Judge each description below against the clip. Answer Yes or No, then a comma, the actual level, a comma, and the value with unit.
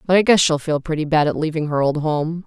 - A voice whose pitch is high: No, medium, 160 Hz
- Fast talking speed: Yes, fast, 290 wpm